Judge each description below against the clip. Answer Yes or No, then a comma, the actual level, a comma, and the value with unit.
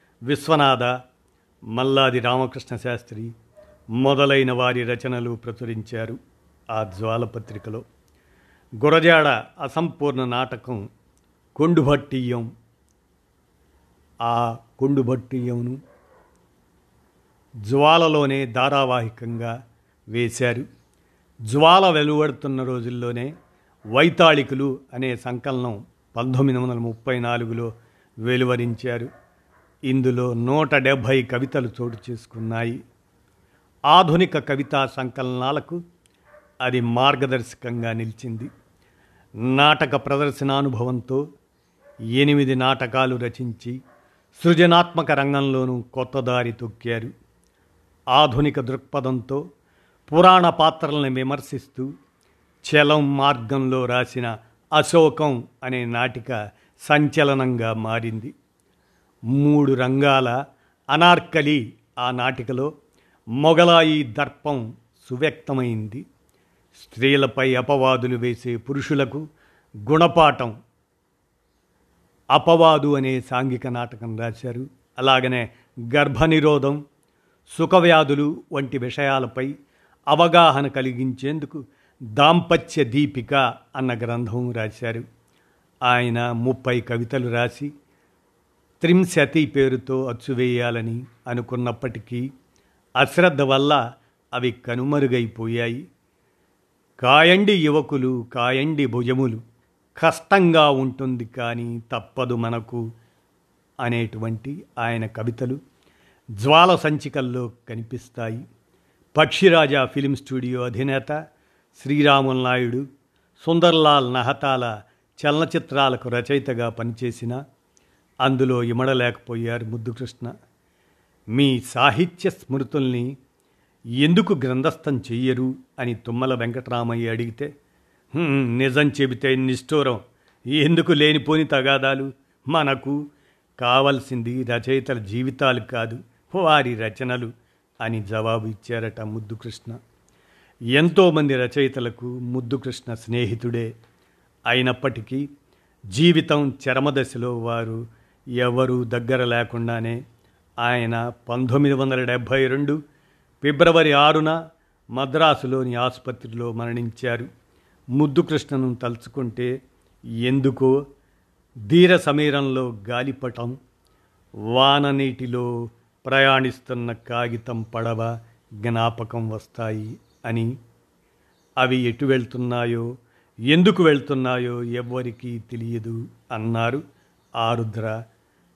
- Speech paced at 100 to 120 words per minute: No, slow, 70 wpm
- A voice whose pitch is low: Yes, low, 125 Hz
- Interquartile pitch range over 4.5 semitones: No, average, 3.0 semitones